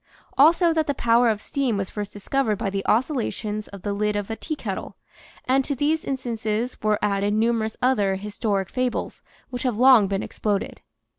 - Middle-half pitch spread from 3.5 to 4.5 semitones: Yes, average, 4.0 semitones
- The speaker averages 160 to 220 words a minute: Yes, average, 175 wpm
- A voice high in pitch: Yes, high, 220 Hz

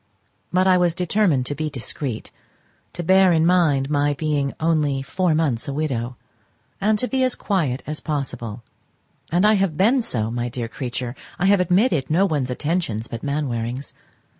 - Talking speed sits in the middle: Yes, average, 170 wpm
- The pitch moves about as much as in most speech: No, wide, 6.0 semitones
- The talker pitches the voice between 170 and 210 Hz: No, medium, 150 Hz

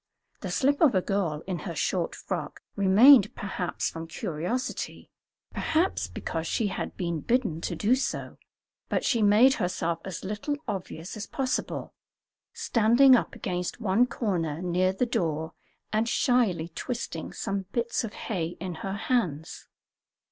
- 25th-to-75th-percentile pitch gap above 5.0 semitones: Yes, wide, 5.6 semitones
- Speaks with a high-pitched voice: Yes, high, 195 Hz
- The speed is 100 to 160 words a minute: Yes, average, 145 wpm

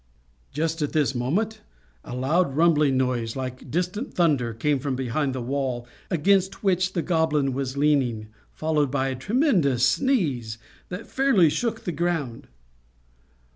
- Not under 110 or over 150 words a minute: Yes, average, 140 wpm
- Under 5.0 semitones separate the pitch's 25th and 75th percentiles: No, average, 5.3 semitones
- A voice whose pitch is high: No, medium, 145 Hz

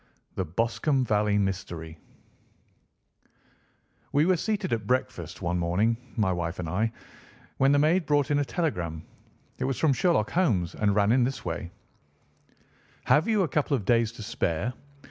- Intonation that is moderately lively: No, wide, 8.1 semitones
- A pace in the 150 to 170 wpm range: Yes, average, 160 wpm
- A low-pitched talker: Yes, low, 115 Hz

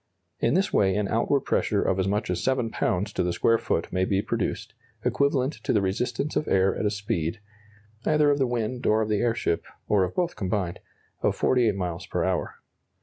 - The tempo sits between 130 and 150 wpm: No, fast, 205 wpm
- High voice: No, low, 105 Hz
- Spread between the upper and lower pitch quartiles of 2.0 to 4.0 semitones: No, average, 4.8 semitones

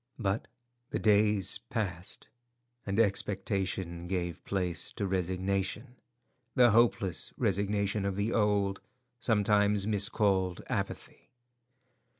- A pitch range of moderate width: No, narrow, 1.9 semitones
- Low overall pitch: Yes, low, 100 Hz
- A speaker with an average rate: No, slow, 90 wpm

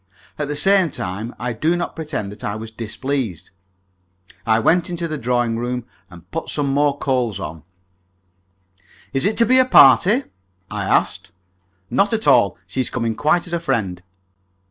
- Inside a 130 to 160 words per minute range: No, average, 170 wpm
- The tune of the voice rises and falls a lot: Yes, wide, 6.9 semitones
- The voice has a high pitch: No, low, 130 Hz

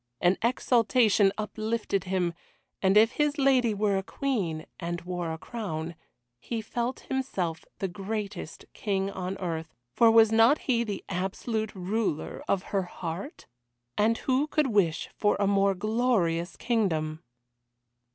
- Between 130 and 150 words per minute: Yes, average, 140 wpm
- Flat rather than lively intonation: No, average, 4.2 semitones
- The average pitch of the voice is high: Yes, high, 205 Hz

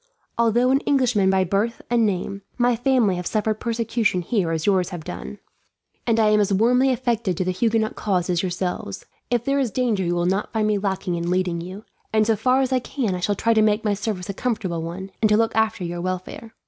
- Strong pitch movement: No, average, 3.9 semitones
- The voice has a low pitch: No, high, 210 Hz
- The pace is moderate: No, fast, 230 wpm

